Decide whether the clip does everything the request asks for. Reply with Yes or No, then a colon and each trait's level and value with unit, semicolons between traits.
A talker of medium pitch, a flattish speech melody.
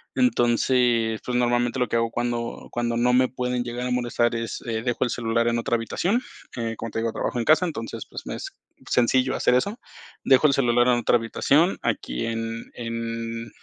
No: low, 120 Hz; narrow, 1.4 semitones